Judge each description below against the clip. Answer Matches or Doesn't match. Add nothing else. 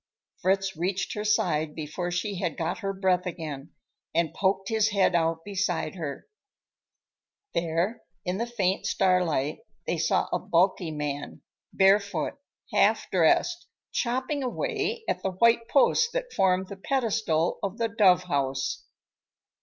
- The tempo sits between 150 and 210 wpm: Doesn't match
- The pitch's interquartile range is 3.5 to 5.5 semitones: Matches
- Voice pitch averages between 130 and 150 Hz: Doesn't match